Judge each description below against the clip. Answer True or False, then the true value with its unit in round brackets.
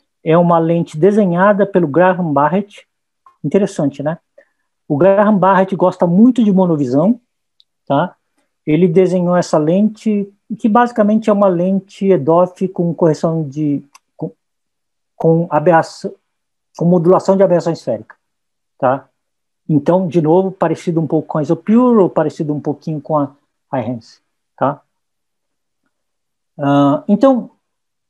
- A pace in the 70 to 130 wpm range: True (125 wpm)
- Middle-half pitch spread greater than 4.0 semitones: False (3.7 semitones)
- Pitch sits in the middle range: True (180 Hz)